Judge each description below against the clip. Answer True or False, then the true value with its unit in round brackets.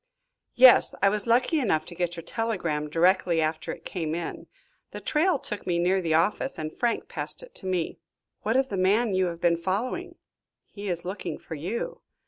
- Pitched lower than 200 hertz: True (185 Hz)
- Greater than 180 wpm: True (195 wpm)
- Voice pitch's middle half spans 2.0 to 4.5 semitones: False (5.1 semitones)